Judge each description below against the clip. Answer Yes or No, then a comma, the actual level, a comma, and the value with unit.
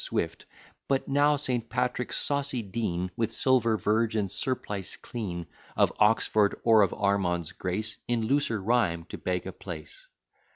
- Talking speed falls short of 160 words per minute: Yes, average, 150 wpm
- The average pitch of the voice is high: No, low, 110 Hz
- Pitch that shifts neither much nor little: Yes, average, 4.2 semitones